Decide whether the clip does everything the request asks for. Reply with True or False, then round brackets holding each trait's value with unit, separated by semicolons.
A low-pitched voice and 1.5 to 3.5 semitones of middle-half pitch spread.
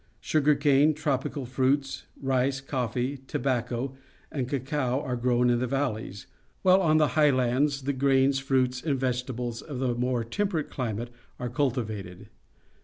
True (130 Hz; 2.4 semitones)